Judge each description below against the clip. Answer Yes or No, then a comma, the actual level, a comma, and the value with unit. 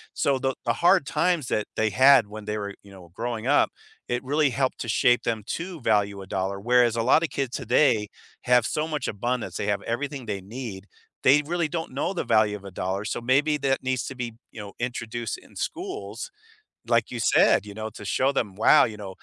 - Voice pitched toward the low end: Yes, low, 120 Hz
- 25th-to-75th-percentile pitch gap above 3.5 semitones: Yes, average, 4.7 semitones